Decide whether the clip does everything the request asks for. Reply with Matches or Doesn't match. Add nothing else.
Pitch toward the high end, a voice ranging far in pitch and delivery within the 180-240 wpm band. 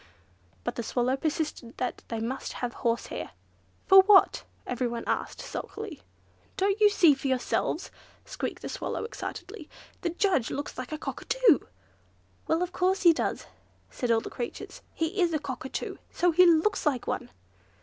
Doesn't match